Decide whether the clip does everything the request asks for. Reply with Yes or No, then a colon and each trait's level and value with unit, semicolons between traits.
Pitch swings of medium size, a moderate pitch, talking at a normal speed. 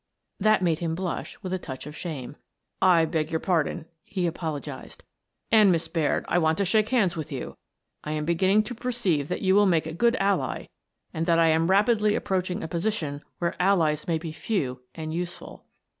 No: average, 3.6 semitones; medium, 170 Hz; fast, 210 wpm